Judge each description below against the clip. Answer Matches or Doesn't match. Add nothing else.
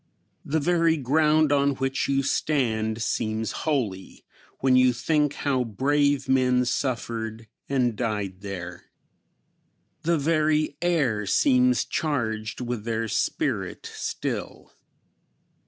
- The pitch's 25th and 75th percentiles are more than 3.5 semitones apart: Matches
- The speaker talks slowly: Matches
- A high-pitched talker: Doesn't match